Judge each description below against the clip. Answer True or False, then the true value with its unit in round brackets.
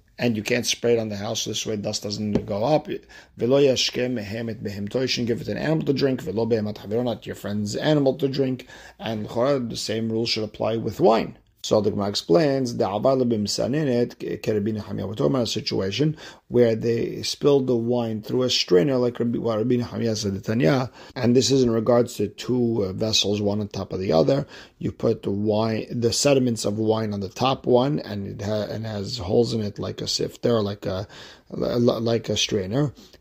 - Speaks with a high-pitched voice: False (115 Hz)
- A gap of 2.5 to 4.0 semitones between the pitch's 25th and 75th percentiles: True (2.8 semitones)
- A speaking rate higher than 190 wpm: False (185 wpm)